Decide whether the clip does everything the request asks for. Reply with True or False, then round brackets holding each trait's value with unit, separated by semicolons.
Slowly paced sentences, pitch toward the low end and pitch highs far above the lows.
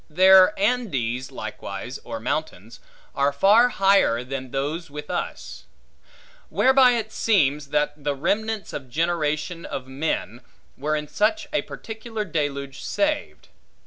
False (125 wpm; 150 Hz; 7.2 semitones)